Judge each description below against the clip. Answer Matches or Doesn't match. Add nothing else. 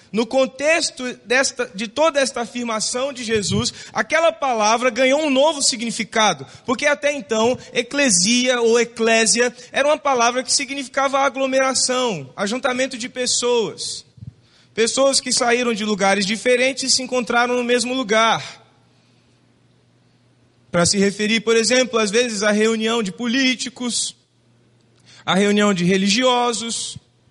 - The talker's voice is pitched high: Matches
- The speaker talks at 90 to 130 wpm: Matches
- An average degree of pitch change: Matches